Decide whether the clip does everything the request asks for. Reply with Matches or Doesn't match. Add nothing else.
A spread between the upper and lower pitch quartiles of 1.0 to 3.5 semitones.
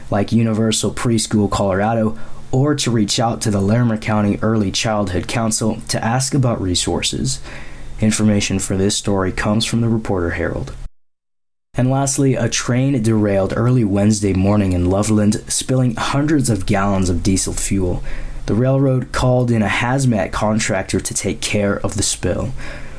Matches